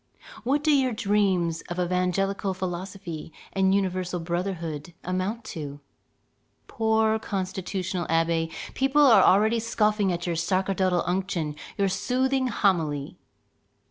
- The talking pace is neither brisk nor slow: No, slow, 110 wpm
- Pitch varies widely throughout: No, average, 3.4 semitones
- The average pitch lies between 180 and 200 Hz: Yes, high, 190 Hz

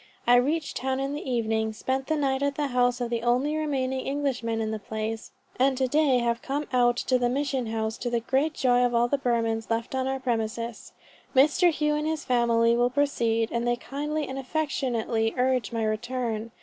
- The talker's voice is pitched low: No, very high, 250 Hz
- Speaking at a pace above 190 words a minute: Yes, fast, 205 wpm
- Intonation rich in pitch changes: No, average, 2.9 semitones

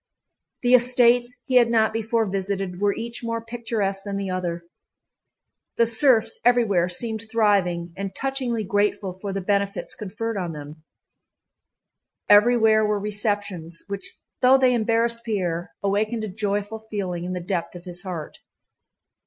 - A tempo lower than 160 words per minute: Yes, average, 145 wpm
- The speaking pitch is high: Yes, high, 205 Hz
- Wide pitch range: No, average, 3.5 semitones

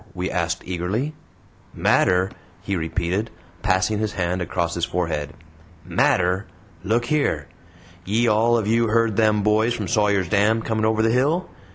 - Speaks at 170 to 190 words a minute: No, average, 150 wpm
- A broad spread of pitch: No, average, 3.7 semitones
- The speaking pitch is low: Yes, low, 105 Hz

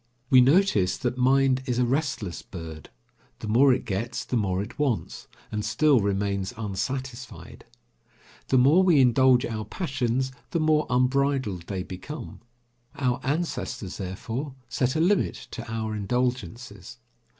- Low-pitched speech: Yes, low, 125 Hz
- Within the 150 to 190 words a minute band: No, average, 140 wpm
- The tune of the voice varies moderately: Yes, average, 4.3 semitones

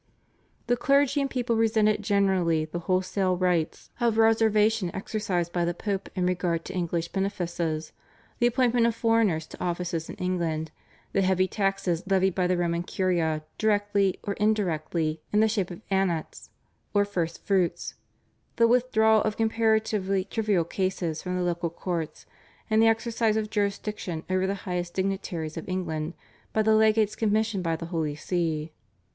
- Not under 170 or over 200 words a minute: No, average, 155 wpm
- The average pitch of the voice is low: No, high, 190 Hz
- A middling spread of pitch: Yes, average, 4.0 semitones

